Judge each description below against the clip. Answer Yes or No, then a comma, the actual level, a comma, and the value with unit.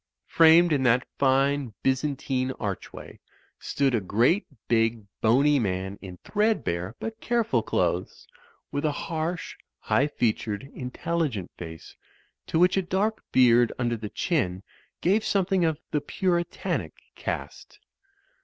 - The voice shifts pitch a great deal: Yes, wide, 7.1 semitones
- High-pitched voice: No, low, 135 Hz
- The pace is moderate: No, slow, 125 wpm